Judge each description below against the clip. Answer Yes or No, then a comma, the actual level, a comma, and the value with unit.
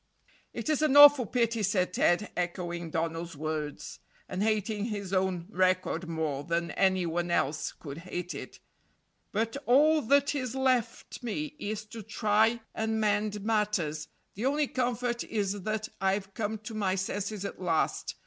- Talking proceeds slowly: No, average, 155 wpm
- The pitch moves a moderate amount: Yes, average, 4.3 semitones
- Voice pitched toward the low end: No, high, 205 Hz